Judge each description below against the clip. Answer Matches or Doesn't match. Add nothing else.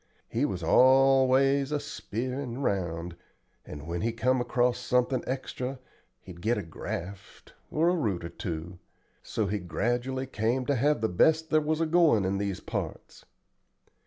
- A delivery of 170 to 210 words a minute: Doesn't match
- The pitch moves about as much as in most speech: Doesn't match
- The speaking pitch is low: Matches